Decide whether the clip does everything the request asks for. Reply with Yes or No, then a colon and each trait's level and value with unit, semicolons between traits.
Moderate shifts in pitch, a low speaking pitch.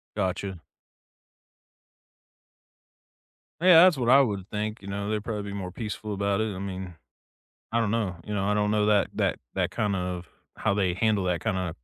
No: narrow, 2.1 semitones; low, 100 Hz